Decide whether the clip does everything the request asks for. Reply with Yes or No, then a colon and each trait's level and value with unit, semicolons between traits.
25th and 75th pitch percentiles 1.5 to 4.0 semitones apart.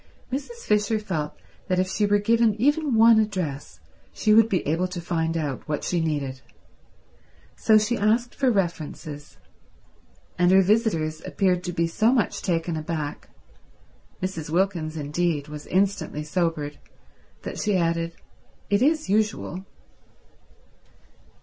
No: average, 5.0 semitones